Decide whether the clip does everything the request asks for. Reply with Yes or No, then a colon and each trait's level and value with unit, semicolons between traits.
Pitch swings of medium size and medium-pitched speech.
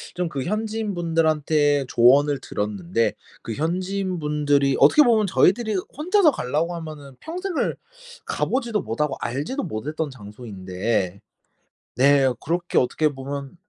No: wide, 5.9 semitones; medium, 150 Hz